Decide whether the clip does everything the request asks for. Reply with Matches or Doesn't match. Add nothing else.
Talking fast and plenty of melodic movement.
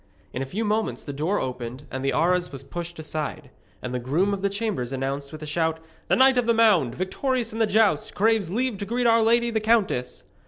Matches